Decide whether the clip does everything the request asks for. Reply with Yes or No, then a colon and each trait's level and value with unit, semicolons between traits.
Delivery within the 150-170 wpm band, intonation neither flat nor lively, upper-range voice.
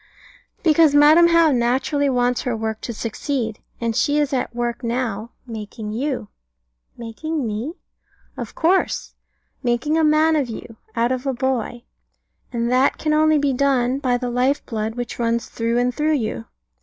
Yes: average, 165 wpm; average, 3.8 semitones; very high, 250 Hz